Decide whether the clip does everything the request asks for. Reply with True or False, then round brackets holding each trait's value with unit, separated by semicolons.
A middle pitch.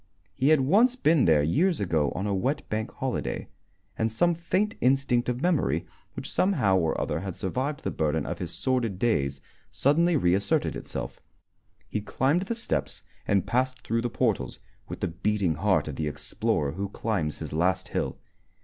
False (110 Hz)